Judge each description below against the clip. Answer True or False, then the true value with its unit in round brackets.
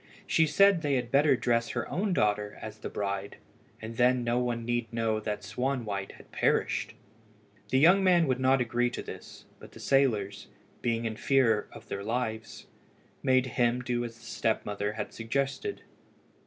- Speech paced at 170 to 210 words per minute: True (175 wpm)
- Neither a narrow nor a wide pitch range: True (3.1 semitones)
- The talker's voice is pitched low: True (120 Hz)